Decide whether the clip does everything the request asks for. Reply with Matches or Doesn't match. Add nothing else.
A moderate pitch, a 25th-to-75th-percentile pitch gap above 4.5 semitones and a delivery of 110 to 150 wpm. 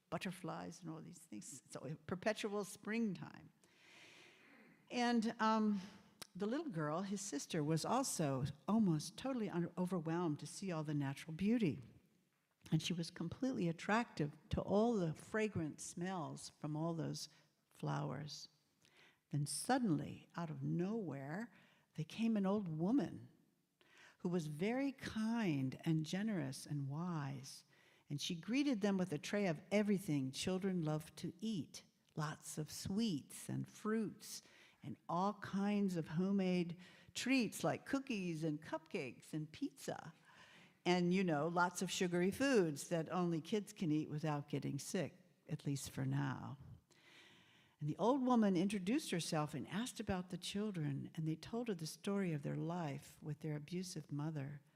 Matches